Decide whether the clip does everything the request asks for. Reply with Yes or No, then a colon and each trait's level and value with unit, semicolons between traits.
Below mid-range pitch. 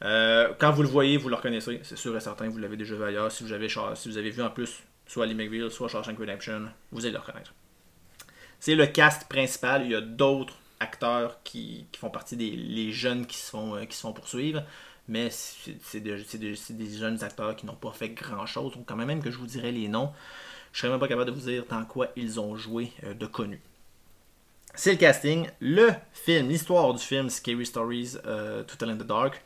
Yes: low, 120 Hz